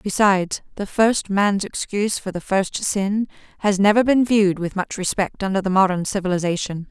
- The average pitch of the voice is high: Yes, high, 195 Hz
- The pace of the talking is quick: No, average, 175 wpm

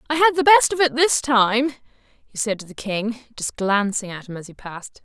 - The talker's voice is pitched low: No, high, 240 Hz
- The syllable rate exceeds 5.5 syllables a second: No, 5.1 syllables/s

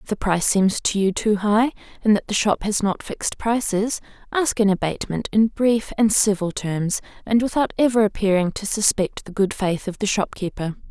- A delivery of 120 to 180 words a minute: No, average, 200 wpm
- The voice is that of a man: No, female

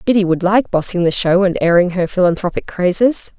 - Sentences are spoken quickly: No, average, 195 wpm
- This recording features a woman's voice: Yes, female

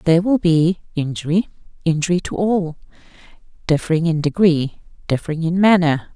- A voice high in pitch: No, medium, 170 Hz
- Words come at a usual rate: No, slow, 115 wpm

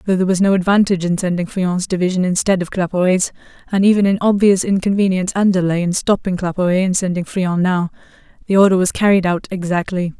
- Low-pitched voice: No, medium, 185 Hz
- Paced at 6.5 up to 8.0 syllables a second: Yes, 6.6 syllables/s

